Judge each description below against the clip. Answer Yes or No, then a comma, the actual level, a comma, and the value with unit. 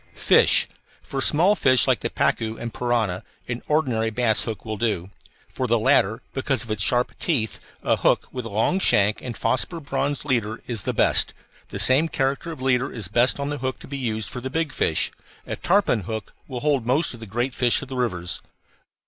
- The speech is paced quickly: Yes, fast, 210 wpm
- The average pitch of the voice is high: No, low, 125 Hz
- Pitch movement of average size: Yes, average, 3.7 semitones